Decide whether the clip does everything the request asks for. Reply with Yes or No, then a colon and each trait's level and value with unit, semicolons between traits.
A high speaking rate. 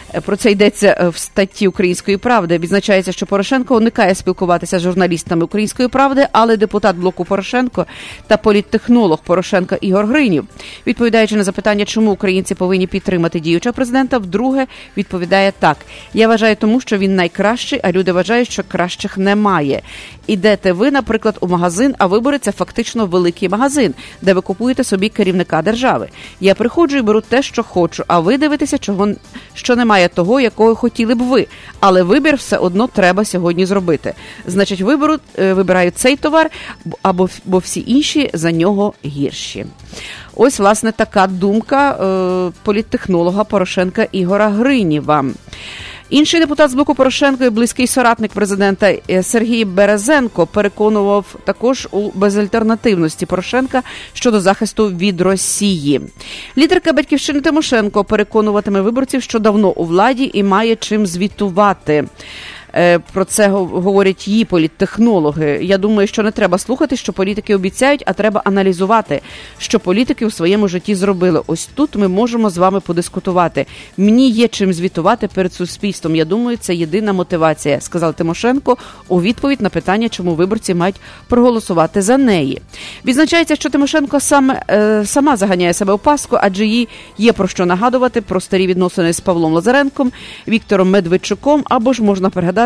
No: average, 145 wpm